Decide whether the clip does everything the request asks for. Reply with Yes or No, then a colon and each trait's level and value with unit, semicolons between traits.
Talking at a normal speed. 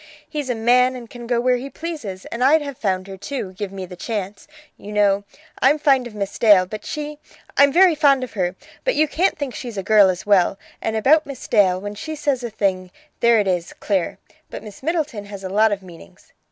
No: fast, 230 wpm